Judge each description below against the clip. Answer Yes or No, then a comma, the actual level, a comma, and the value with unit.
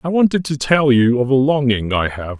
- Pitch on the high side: No, low, 135 Hz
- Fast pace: Yes, fast, 250 wpm